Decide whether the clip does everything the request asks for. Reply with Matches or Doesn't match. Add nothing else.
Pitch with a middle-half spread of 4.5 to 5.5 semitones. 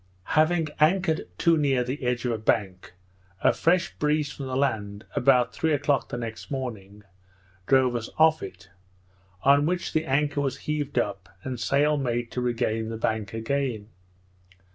Matches